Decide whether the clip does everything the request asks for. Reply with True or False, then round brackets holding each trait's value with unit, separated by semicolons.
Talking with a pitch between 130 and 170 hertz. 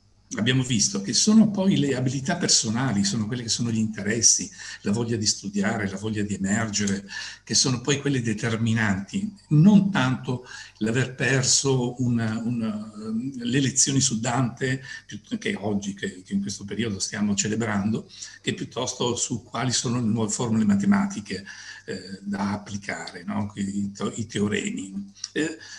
False (115 Hz)